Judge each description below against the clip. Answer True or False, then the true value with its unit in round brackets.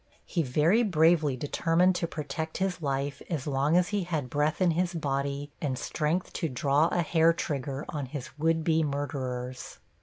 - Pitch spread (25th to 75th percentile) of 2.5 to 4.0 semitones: True (3.3 semitones)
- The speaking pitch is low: False (150 Hz)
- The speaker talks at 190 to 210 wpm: False (175 wpm)